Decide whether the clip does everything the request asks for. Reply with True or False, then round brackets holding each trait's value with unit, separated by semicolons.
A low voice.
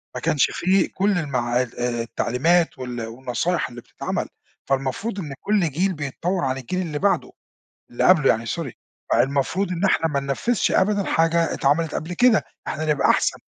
False (155 Hz)